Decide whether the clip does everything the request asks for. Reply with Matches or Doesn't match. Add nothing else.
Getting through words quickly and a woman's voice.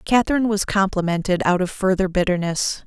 Doesn't match